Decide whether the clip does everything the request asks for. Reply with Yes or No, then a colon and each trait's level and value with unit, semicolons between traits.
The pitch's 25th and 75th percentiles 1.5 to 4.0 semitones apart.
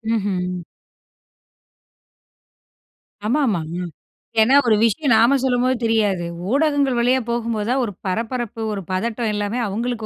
Yes: average, 3.4 semitones